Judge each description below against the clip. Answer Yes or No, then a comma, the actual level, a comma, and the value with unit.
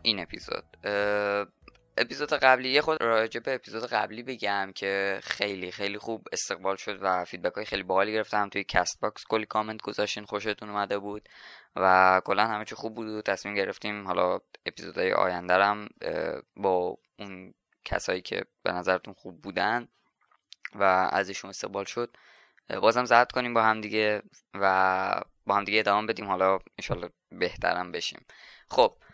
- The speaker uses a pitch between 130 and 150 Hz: No, low, 100 Hz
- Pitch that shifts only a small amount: Yes, narrow, 2.2 semitones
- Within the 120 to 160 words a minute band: Yes, average, 150 wpm